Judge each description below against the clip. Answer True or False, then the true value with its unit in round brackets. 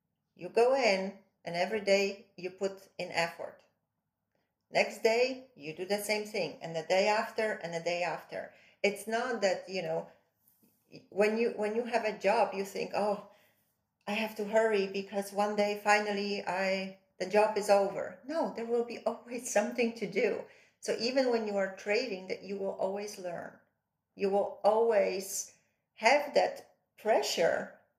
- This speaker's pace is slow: False (165 wpm)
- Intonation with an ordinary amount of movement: False (2.3 semitones)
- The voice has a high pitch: True (205 Hz)